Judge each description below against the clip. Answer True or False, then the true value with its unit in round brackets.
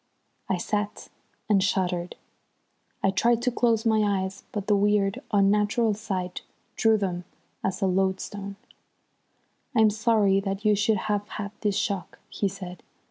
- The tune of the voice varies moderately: False (1.8 semitones)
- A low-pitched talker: False (200 Hz)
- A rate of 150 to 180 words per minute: False (140 wpm)